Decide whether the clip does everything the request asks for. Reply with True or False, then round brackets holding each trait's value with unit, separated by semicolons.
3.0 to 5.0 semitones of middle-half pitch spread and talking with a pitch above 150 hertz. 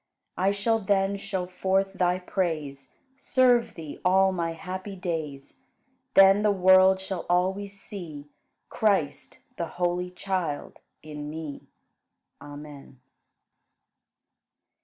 True (3.4 semitones; 185 Hz)